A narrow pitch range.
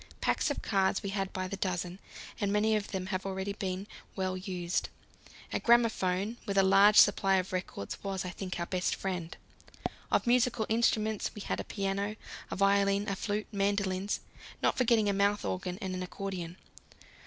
Yes: narrow, 1.8 semitones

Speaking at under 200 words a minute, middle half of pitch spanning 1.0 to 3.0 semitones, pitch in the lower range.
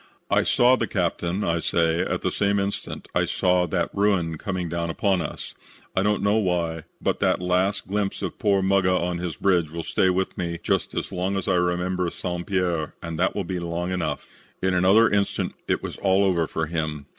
No: fast, 205 wpm; narrow, 2.4 semitones; very low, 90 Hz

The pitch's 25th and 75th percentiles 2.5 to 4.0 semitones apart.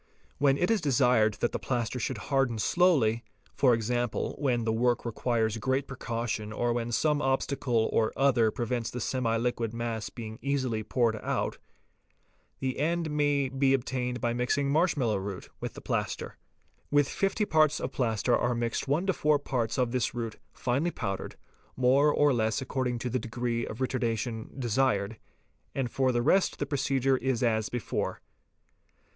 Yes: average, 2.9 semitones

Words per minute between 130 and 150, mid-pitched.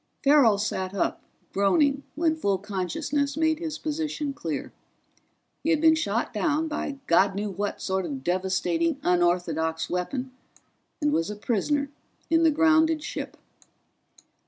No: slow, 135 wpm; very high, 265 Hz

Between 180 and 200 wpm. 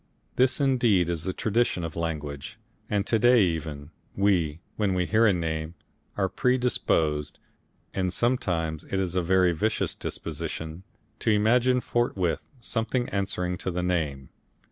No: average, 145 wpm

